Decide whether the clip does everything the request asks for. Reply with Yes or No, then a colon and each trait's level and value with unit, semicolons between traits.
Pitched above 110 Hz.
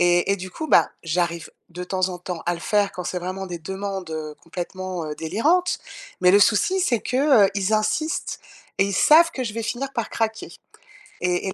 Yes: high, 190 Hz